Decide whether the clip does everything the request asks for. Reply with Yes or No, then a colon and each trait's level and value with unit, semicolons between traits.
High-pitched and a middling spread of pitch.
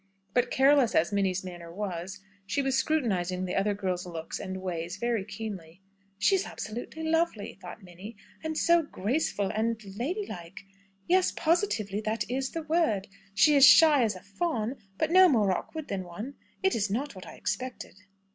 No: high, 215 Hz; wide, 7.2 semitones